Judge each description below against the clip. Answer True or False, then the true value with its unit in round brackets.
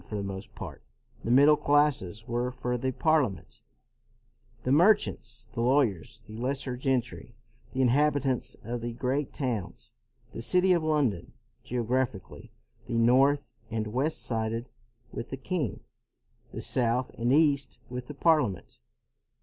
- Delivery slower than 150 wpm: True (135 wpm)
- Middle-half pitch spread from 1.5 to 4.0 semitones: True (3.6 semitones)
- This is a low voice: True (125 Hz)